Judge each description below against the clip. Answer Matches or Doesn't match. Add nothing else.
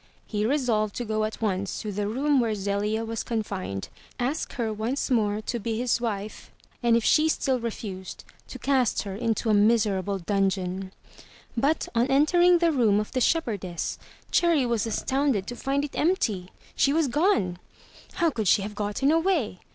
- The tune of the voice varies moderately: Matches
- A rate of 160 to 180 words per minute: Matches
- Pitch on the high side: Matches